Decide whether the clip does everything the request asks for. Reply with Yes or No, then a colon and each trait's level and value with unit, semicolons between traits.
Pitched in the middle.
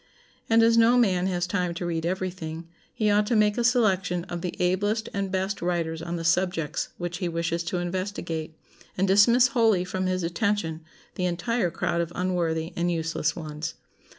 Yes: medium, 180 Hz